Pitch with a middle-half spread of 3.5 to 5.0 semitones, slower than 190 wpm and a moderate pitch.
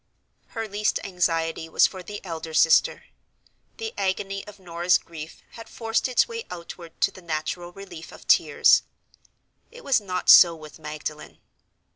Yes: average, 4.1 semitones; average, 150 wpm; medium, 180 Hz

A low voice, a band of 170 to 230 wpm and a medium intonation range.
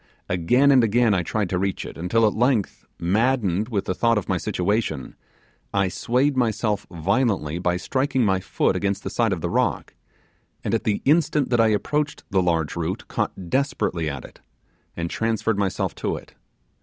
Yes: low, 105 Hz; average, 180 wpm; average, 5.0 semitones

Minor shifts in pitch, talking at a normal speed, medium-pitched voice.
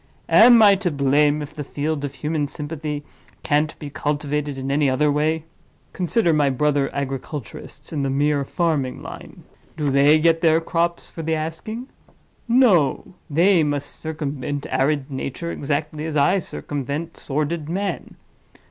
Yes: narrow, 2.3 semitones; average, 145 wpm; medium, 150 Hz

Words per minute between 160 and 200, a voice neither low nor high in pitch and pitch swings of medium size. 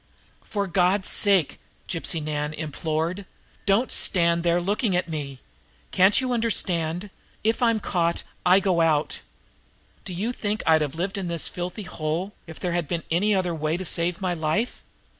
Yes: average, 165 wpm; medium, 175 Hz; average, 3.5 semitones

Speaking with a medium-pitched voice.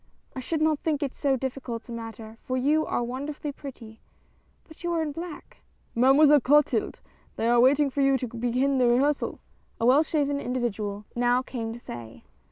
No: very high, 260 Hz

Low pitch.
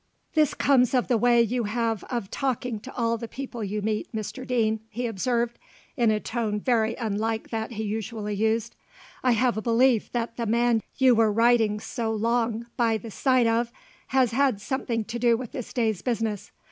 No: high, 230 Hz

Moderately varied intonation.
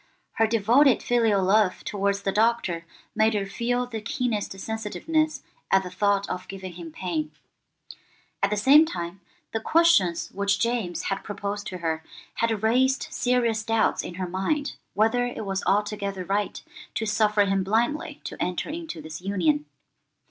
Yes: average, 3.5 semitones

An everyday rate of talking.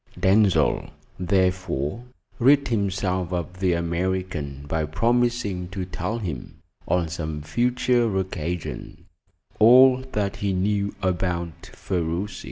No: slow, 105 wpm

